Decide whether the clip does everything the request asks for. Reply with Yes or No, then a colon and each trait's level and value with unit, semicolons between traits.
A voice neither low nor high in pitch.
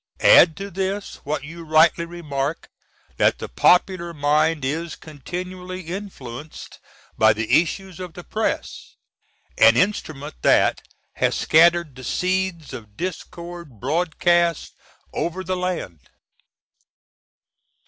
Yes: medium, 170 Hz